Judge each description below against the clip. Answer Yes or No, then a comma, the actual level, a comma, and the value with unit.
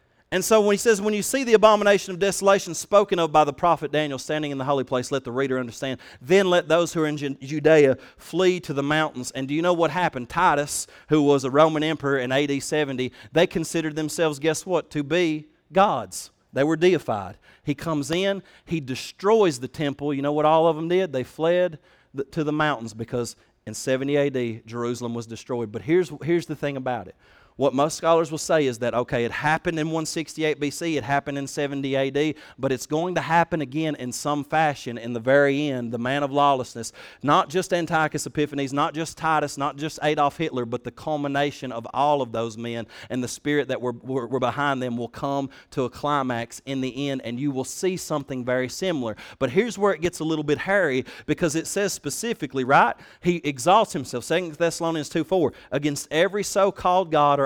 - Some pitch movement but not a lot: Yes, average, 3.7 semitones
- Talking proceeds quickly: Yes, fast, 210 wpm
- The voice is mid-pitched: Yes, medium, 145 Hz